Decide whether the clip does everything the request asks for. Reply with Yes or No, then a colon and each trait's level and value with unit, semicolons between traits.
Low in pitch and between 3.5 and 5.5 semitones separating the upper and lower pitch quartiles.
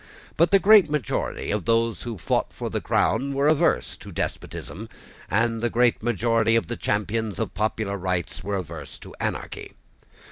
No: low, 115 Hz; average, 2.9 semitones